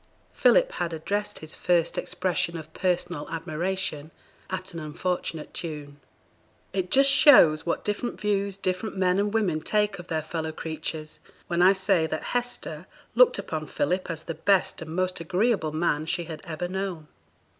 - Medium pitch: Yes, medium, 180 Hz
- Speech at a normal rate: Yes, average, 160 wpm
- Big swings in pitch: No, average, 3.7 semitones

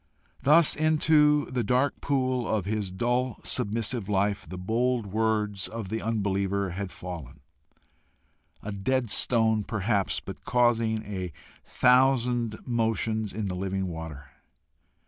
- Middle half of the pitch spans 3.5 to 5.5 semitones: Yes, average, 4.0 semitones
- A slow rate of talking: Yes, slow, 125 wpm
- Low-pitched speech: Yes, low, 110 Hz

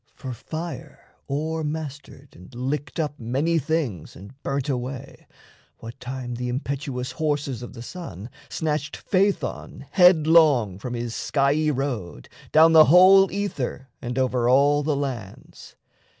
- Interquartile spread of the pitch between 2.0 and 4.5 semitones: Yes, average, 4.1 semitones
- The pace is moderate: No, slow, 130 wpm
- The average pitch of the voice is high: No, medium, 140 Hz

